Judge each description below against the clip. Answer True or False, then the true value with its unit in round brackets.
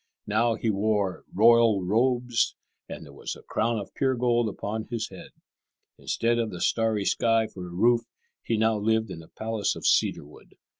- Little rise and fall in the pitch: True (2.3 semitones)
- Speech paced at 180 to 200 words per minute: True (185 wpm)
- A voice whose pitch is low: True (110 Hz)